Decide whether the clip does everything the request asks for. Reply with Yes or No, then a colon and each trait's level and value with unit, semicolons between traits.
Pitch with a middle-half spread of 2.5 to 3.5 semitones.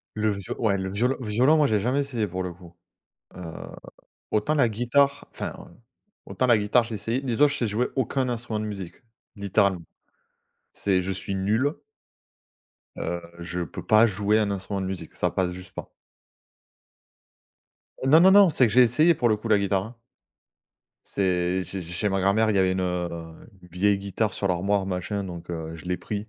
No: average, 4.1 semitones